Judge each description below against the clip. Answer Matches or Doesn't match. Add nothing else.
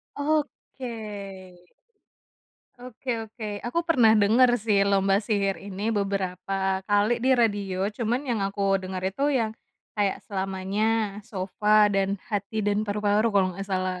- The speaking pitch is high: Matches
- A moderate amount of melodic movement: Doesn't match